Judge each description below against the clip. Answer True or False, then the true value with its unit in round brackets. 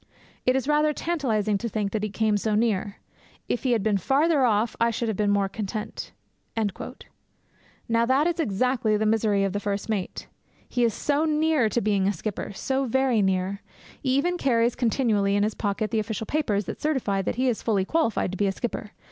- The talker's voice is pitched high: True (220 Hz)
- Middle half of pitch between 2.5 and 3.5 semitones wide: False (4.2 semitones)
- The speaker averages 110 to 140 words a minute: False (205 wpm)